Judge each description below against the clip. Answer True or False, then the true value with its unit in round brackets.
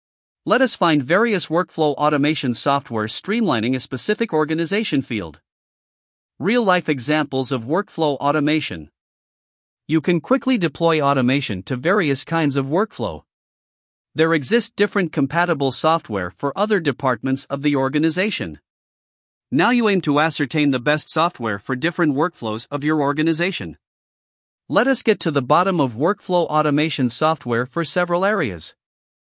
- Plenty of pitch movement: False (4.9 semitones)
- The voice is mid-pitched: True (150 Hz)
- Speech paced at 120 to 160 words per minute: True (135 wpm)